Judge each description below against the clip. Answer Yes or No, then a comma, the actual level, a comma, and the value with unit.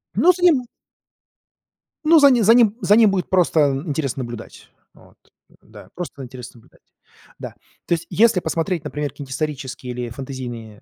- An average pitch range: No, wide, 8.6 semitones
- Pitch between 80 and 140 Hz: No, medium, 155 Hz